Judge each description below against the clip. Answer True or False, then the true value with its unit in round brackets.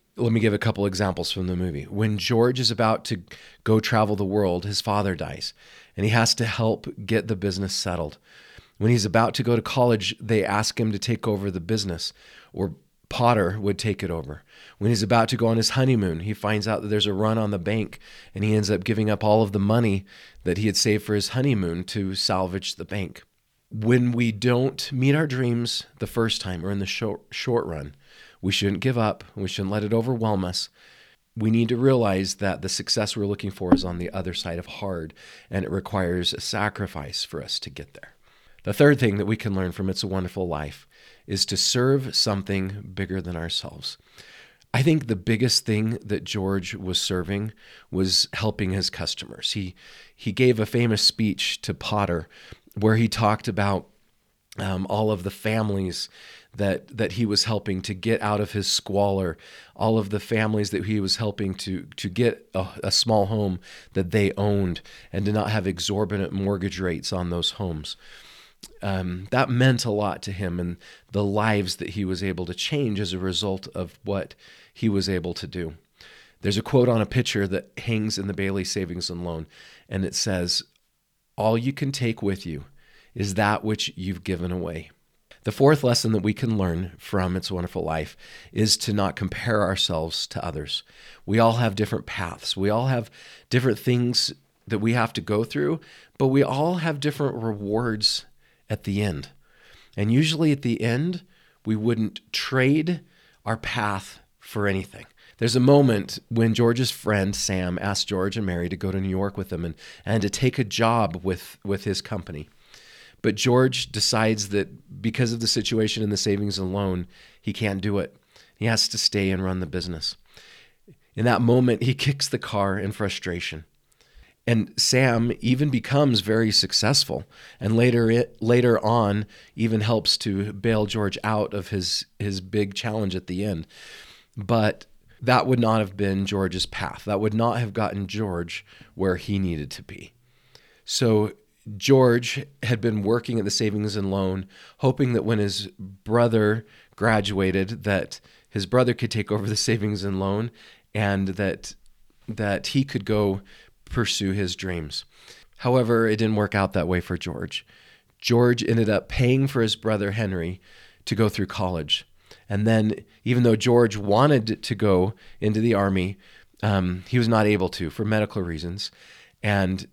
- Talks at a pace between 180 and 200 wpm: True (185 wpm)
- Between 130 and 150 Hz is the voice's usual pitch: False (105 Hz)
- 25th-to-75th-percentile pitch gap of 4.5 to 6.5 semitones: False (3.1 semitones)